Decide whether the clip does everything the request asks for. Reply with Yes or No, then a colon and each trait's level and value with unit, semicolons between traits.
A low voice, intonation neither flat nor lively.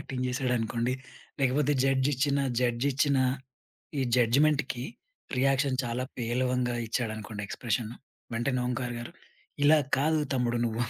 No: low, 125 Hz; narrow, 2.2 semitones